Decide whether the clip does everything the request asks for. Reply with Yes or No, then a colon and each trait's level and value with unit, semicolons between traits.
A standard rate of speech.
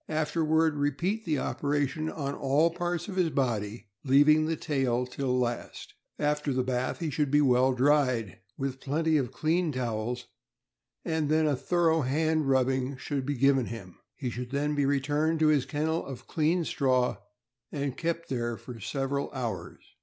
Yes: average, 170 wpm